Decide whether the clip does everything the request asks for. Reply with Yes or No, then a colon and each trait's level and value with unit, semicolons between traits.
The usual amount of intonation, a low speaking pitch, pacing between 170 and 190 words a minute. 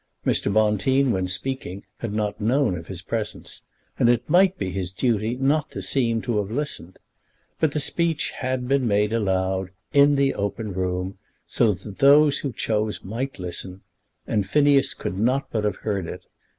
No: wide, 5.9 semitones; low, 110 Hz; average, 175 wpm